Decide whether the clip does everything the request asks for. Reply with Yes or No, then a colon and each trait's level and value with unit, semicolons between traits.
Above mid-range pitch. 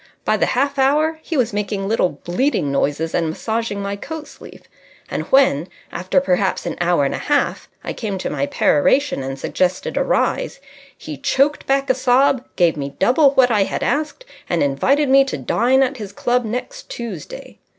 Yes: high, 235 Hz